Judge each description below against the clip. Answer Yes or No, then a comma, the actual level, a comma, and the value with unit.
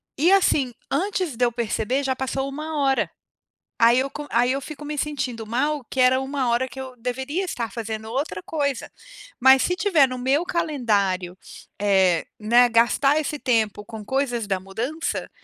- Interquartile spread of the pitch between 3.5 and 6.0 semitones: Yes, average, 3.9 semitones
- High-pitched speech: Yes, very high, 260 Hz